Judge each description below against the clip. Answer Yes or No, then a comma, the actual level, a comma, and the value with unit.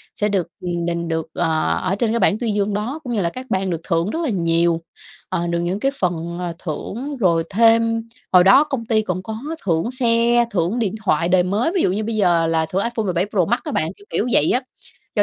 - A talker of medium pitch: No, high, 195 Hz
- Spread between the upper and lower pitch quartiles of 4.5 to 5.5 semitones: Yes, average, 5.1 semitones